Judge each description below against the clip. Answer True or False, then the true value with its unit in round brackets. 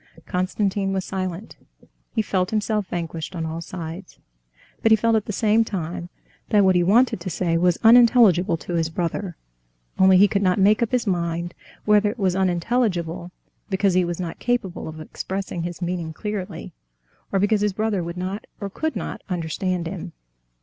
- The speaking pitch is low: False (185 Hz)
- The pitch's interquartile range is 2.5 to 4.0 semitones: True (3.3 semitones)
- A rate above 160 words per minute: True (175 wpm)